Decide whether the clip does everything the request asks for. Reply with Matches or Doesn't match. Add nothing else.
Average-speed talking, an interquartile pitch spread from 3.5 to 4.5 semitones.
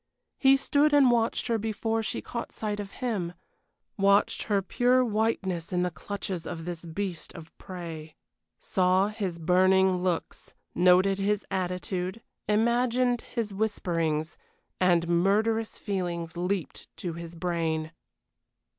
Doesn't match